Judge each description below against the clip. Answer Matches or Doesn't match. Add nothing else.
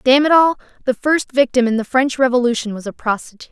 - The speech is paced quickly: Matches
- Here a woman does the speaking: Matches